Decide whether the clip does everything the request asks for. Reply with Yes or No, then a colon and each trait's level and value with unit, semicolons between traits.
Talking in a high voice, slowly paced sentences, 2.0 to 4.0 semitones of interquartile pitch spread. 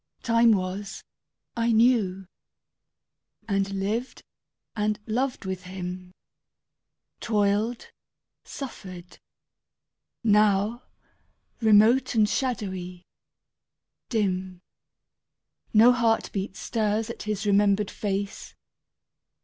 Yes: high, 210 Hz; slow, 75 wpm; average, 2.9 semitones